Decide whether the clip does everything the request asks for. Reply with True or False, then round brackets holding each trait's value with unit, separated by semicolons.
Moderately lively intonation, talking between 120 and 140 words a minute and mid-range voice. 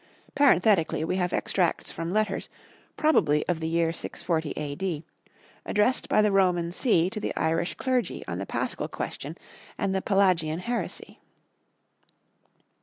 True (4.1 semitones; 135 wpm; 180 Hz)